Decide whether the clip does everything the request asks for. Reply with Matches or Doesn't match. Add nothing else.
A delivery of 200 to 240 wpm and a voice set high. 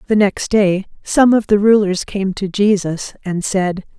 Doesn't match